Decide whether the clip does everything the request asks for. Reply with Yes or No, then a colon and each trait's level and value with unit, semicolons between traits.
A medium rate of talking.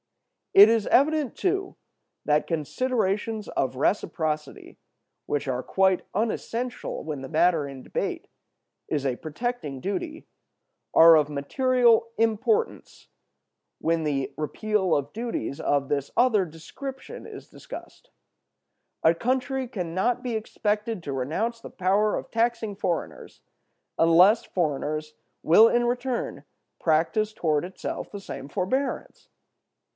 No: slow, 120 wpm